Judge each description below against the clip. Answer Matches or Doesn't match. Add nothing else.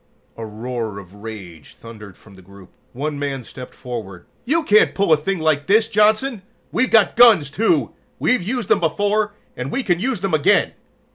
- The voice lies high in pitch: Doesn't match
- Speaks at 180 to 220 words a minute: Matches